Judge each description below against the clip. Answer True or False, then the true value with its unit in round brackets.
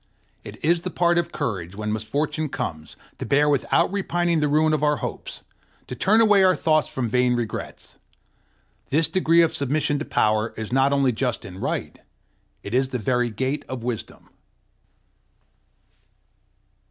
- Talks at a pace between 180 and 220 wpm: False (160 wpm)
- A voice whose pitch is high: False (140 Hz)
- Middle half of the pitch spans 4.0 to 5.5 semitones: True (4.8 semitones)